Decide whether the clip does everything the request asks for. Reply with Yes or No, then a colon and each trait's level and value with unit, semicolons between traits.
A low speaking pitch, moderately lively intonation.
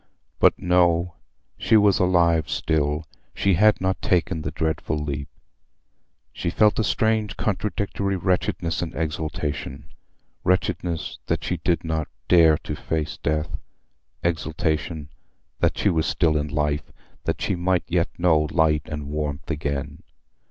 Yes: very low, 80 Hz; average, 3.0 semitones